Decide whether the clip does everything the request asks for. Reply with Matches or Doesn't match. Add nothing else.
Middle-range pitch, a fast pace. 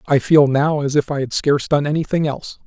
Matches